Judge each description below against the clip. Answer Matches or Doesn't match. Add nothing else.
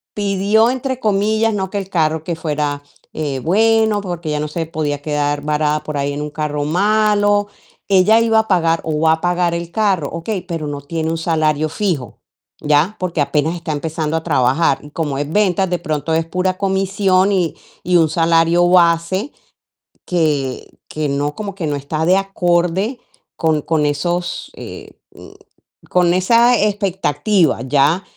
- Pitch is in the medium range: Matches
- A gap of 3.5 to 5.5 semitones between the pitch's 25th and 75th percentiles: Matches